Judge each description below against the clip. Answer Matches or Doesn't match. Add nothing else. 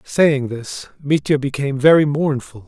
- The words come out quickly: Doesn't match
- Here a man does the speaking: Matches